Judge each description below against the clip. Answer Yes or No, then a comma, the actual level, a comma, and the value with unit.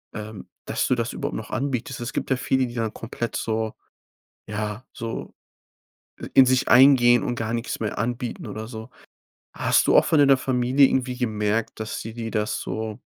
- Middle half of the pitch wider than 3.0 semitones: No, narrow, 2.6 semitones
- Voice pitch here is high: No, low, 120 Hz